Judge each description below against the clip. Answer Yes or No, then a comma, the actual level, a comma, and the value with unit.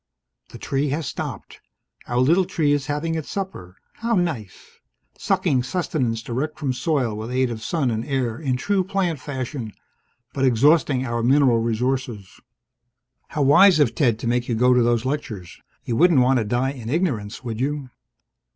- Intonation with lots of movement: No, average, 4.2 semitones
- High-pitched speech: No, low, 130 Hz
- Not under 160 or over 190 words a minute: Yes, average, 170 wpm